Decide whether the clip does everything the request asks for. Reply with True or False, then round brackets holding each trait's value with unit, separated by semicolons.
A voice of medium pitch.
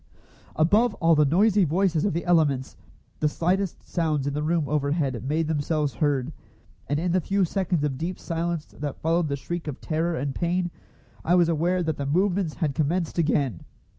True (160 Hz)